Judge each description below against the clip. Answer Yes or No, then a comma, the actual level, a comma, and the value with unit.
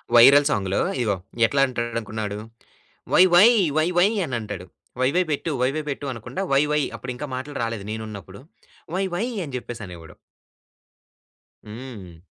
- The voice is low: Yes, low, 120 Hz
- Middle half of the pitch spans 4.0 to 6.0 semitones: Yes, wide, 5.4 semitones